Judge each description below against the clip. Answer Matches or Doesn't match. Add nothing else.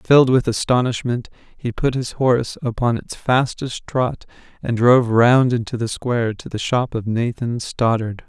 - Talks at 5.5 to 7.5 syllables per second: Doesn't match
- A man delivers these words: Matches